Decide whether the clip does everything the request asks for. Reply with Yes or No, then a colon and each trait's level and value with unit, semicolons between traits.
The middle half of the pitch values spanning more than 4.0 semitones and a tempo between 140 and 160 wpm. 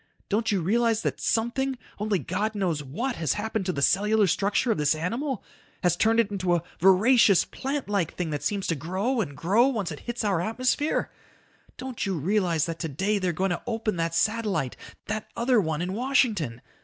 No: average, 5.0 semitones; average, 190 wpm